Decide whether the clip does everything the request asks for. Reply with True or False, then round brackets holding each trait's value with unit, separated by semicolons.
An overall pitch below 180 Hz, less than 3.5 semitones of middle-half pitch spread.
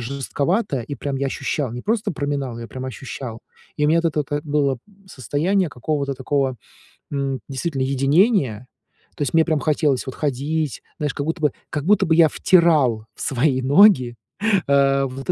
True (140 Hz; 2.9 semitones)